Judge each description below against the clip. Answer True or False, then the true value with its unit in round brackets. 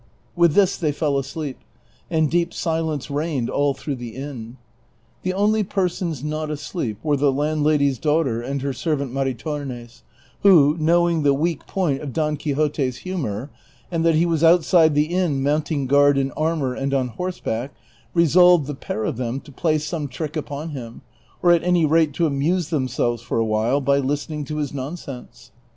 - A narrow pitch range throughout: False (3.2 semitones)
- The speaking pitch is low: False (150 Hz)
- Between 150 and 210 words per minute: True (175 wpm)